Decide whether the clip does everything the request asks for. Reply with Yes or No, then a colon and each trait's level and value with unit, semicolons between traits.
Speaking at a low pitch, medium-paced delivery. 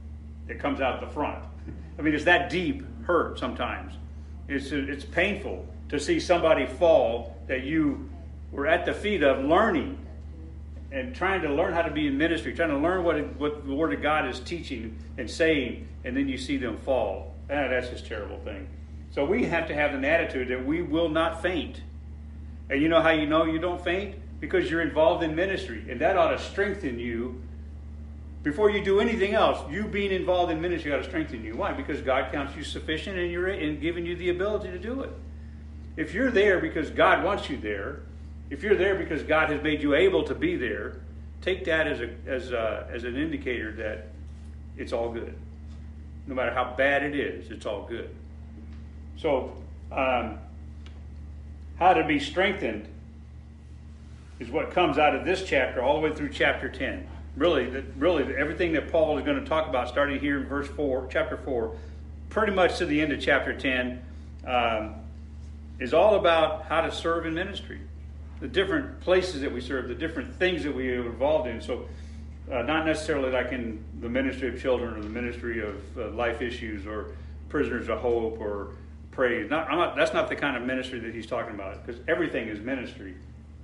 Yes: very low, 75 Hz; average, 195 wpm